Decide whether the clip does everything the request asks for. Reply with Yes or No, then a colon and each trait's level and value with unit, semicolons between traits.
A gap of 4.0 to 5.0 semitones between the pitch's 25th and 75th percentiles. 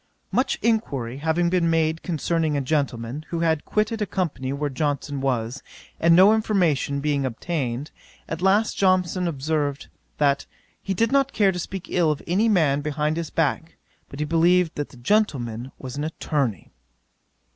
Yes: average, 4.4 semitones